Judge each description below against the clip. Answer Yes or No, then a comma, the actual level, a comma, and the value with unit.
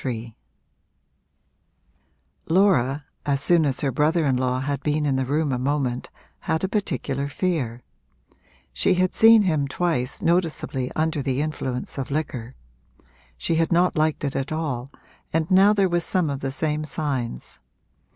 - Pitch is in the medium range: Yes, medium, 150 Hz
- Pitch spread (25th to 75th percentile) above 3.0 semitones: Yes, average, 3.8 semitones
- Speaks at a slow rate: No, average, 155 wpm